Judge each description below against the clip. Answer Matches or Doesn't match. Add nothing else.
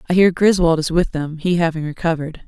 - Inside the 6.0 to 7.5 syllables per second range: Matches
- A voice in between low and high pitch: Matches